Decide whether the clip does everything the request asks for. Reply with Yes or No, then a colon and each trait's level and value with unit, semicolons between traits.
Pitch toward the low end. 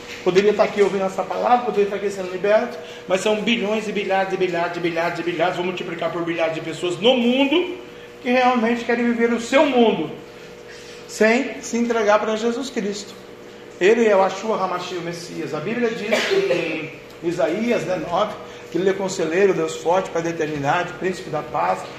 No: high, 190 Hz